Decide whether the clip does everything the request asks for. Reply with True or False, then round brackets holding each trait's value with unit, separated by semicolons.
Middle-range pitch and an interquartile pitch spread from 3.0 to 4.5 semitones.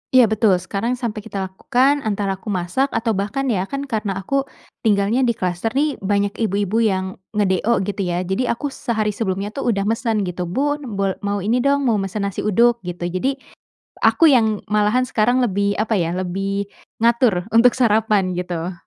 False (210 Hz; 3.5 semitones)